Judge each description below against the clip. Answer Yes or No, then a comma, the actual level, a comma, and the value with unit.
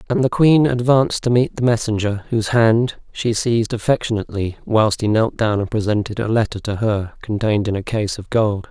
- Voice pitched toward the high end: No, low, 110 Hz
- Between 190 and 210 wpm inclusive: Yes, average, 200 wpm